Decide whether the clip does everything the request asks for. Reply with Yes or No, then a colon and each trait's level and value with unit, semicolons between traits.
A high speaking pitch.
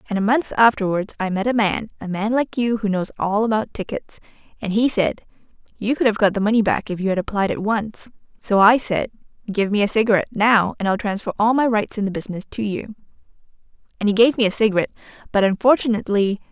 Yes: high, 210 Hz